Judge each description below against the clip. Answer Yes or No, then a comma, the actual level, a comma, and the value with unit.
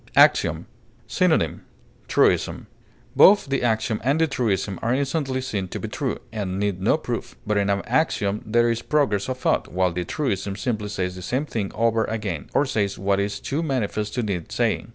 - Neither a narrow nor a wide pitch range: Yes, average, 4.7 semitones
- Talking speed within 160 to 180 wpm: No, average, 190 wpm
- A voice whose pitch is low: Yes, low, 110 Hz